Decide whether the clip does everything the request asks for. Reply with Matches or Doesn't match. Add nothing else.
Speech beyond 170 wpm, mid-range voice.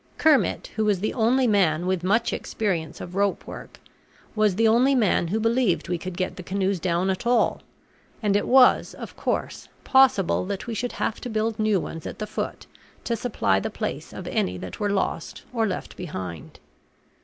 Doesn't match